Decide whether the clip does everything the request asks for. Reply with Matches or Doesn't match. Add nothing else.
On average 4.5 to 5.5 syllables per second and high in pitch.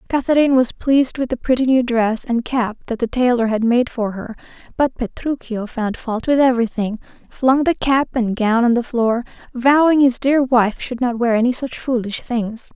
Matches